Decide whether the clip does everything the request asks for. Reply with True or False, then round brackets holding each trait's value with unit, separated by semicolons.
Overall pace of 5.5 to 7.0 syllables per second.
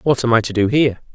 False (7.4 syllables/s)